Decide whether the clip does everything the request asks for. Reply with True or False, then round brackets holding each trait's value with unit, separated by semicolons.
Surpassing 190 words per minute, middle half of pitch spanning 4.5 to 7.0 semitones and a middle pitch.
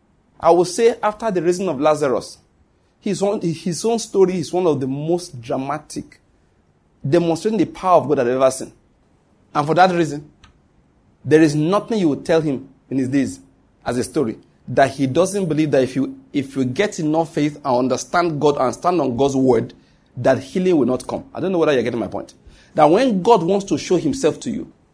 True (205 wpm; 5.1 semitones; 155 Hz)